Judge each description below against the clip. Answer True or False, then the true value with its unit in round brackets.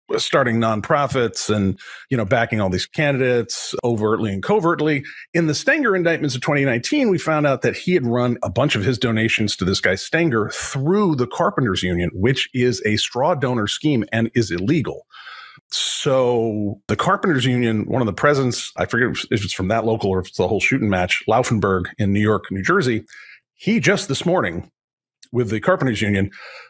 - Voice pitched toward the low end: True (120 Hz)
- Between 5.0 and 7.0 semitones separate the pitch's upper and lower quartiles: True (5.6 semitones)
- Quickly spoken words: False (185 wpm)